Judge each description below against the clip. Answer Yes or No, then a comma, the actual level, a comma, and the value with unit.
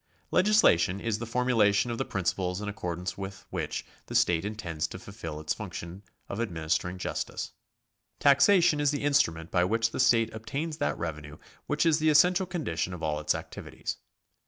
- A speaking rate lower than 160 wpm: No, average, 175 wpm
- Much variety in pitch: Yes, wide, 8.4 semitones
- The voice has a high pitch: No, low, 105 Hz